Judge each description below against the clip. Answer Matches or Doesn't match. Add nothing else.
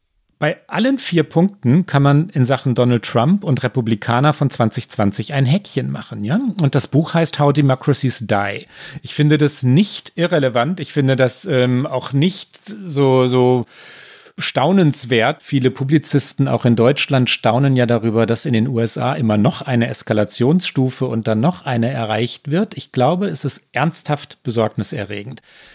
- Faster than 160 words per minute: Doesn't match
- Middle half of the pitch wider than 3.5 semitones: Matches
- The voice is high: Doesn't match